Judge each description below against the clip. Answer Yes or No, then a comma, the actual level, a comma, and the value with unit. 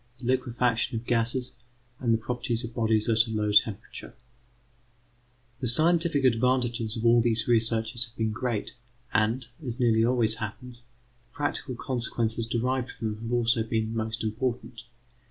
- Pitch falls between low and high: No, low, 115 Hz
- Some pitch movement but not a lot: No, narrow, 1.9 semitones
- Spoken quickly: No, average, 155 wpm